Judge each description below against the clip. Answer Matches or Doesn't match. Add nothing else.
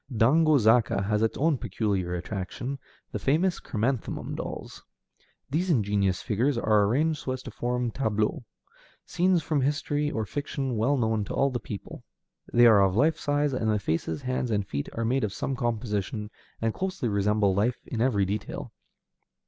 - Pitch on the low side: Matches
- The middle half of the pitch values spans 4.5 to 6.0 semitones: Matches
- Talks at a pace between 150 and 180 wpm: Matches